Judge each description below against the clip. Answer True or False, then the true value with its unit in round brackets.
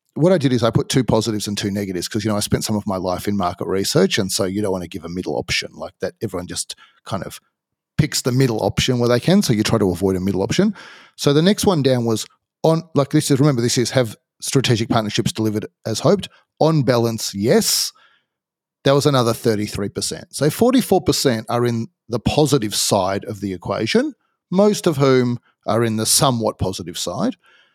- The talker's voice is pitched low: True (120 Hz)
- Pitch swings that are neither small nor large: False (5.8 semitones)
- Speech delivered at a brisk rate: True (215 wpm)